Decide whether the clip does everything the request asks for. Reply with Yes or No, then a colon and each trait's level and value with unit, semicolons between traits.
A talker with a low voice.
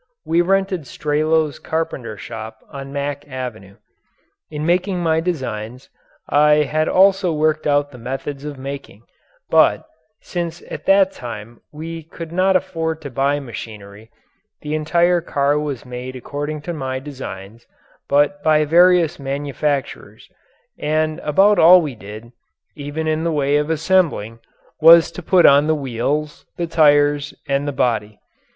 No: medium, 150 Hz